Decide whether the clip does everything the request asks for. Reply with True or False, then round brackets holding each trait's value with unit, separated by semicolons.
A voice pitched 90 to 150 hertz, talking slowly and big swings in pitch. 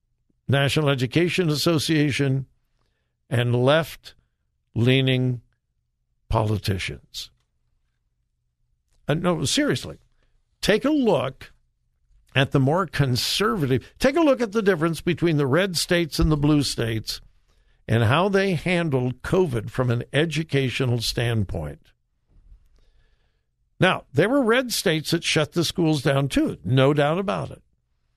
True (135 Hz; 115 wpm; 6.0 semitones)